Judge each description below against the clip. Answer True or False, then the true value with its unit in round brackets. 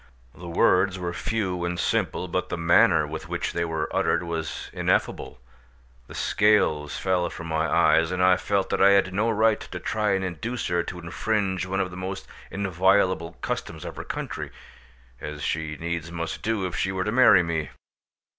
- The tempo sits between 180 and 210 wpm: True (185 wpm)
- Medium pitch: False (90 Hz)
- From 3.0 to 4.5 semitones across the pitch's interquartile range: False (2.6 semitones)